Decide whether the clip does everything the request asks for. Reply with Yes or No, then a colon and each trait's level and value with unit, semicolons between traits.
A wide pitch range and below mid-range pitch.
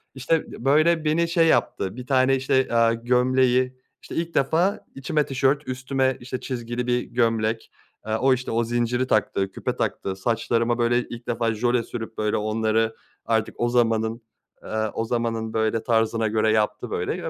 No: average, 2.7 semitones; low, 120 Hz